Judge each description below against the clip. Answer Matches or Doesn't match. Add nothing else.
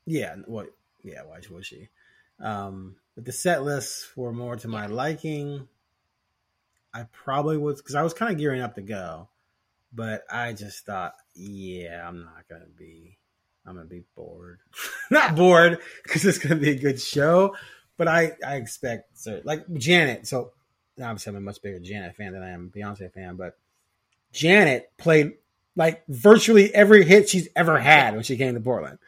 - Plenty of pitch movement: Matches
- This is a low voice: Matches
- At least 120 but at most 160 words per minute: Doesn't match